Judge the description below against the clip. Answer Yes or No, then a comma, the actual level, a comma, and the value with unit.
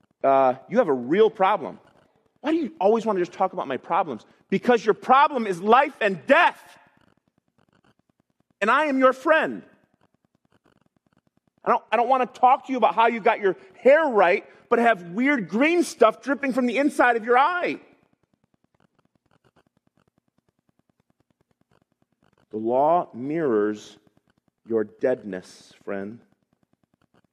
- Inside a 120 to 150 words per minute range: Yes, average, 140 wpm